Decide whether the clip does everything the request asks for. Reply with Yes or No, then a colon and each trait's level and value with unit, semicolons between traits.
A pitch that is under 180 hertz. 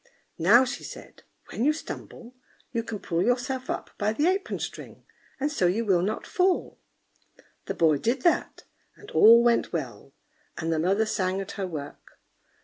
No: high, 220 Hz